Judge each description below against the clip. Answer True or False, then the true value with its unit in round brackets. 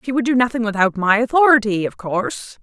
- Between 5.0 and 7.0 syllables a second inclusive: True (6.0 syllables/s)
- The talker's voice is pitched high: True (225 Hz)